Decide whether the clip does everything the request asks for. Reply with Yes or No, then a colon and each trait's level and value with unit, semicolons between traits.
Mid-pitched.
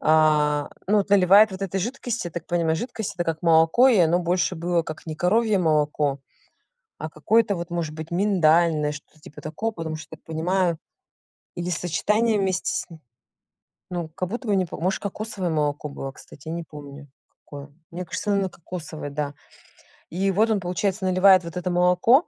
Yes: medium, 175 Hz